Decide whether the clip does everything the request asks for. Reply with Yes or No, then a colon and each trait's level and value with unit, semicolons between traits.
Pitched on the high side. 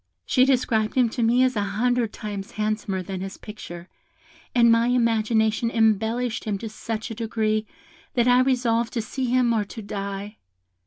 Yes: high, 225 Hz